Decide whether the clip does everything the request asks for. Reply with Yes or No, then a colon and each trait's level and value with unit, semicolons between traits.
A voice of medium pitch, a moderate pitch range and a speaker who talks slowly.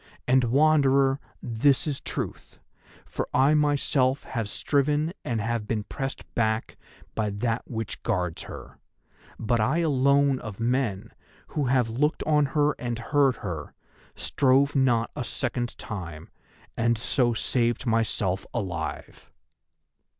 No: low, 125 Hz; average, 3.7 semitones; slow, 130 wpm